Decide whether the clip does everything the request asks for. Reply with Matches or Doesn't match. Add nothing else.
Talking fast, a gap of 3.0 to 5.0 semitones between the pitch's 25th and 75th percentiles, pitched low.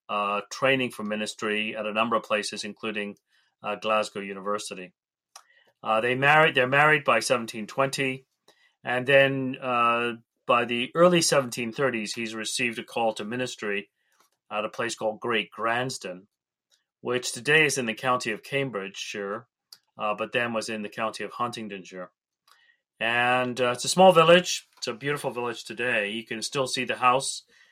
Doesn't match